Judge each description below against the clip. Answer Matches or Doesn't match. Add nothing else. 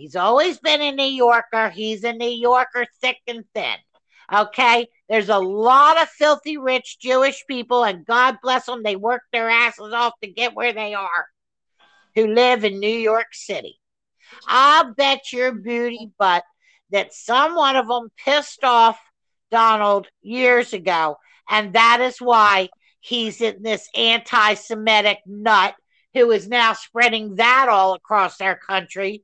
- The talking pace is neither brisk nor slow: Matches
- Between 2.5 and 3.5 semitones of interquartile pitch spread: Matches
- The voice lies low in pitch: Doesn't match